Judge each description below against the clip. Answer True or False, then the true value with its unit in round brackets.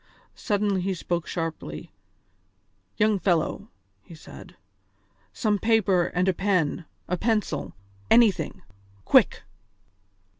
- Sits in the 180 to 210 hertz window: True (190 Hz)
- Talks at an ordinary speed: False (100 wpm)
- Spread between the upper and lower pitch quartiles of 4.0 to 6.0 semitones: False (3.4 semitones)